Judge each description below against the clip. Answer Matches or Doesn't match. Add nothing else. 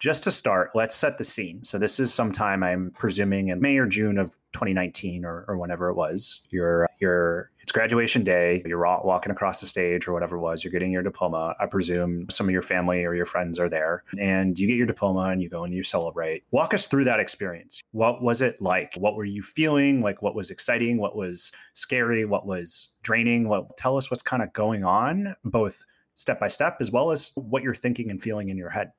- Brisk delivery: Matches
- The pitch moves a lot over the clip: Doesn't match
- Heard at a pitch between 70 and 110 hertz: Matches